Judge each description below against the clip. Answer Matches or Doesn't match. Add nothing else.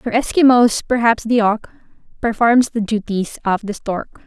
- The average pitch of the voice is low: Doesn't match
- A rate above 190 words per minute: Doesn't match